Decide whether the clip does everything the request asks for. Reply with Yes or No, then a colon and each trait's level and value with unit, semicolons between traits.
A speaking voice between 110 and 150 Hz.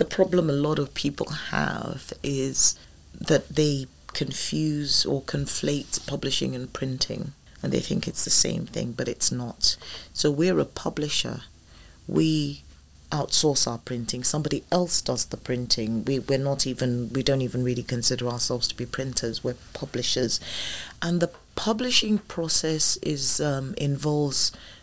Yes: low, 135 Hz